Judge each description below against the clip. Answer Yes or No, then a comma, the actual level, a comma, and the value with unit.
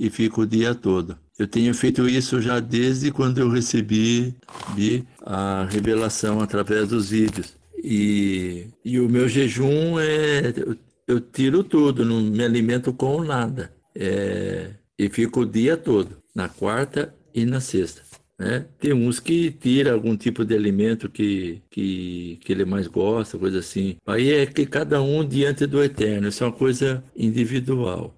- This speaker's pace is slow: No, average, 160 wpm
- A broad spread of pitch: No, average, 3.9 semitones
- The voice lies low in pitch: Yes, low, 120 Hz